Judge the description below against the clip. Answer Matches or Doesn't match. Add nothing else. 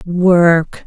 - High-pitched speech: Doesn't match